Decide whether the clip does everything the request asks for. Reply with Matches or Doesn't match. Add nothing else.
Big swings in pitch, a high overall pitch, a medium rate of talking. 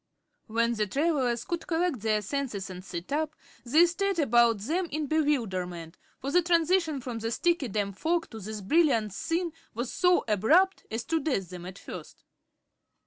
Matches